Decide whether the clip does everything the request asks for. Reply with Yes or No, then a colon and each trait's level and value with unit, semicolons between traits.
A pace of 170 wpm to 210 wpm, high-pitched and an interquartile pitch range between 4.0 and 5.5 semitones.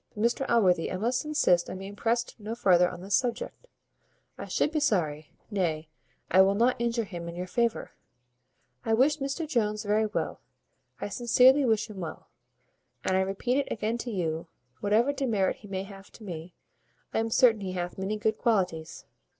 Yes: average, 185 wpm; high, 210 Hz; average, 4.3 semitones